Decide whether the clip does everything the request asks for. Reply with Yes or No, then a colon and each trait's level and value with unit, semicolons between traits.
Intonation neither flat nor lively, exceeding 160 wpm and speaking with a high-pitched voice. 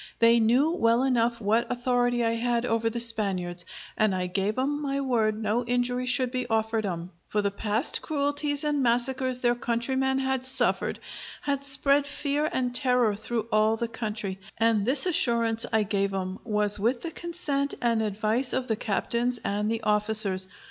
Yes: average, 3.3 semitones; average, 175 wpm; high, 235 Hz